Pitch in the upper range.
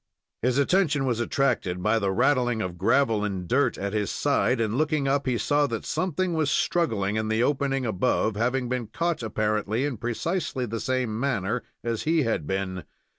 No: low, 120 Hz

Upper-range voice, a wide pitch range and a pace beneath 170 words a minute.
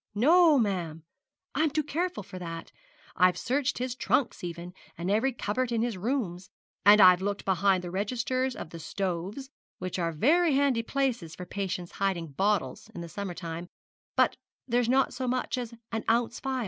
No: high, 205 Hz; wide, 6.2 semitones; average, 175 wpm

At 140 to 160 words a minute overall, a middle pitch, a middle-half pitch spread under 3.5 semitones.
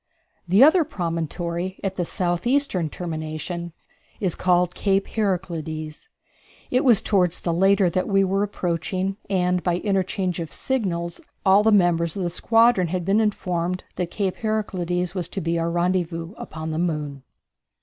Yes: average, 150 wpm; medium, 180 Hz; narrow, 2.6 semitones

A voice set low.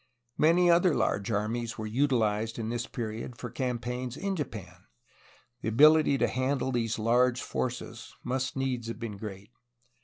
Yes: low, 120 Hz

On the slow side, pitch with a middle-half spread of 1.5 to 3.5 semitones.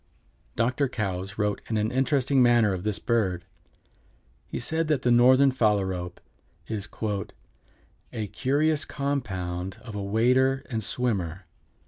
No: slow, 125 wpm; average, 4.9 semitones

